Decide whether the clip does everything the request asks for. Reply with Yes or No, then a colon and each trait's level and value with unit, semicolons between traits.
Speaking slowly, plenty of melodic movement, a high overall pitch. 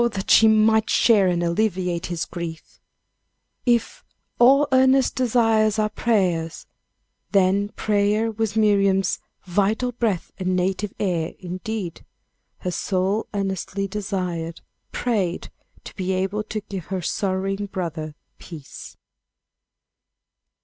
No: slow, 110 wpm; average, 3.2 semitones; high, 195 Hz